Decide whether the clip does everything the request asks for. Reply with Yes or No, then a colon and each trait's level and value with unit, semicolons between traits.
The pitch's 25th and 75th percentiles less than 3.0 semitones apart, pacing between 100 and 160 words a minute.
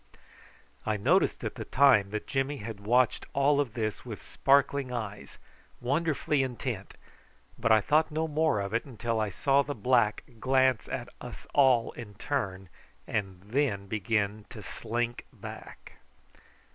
No: average, 4.8 semitones; average, 145 wpm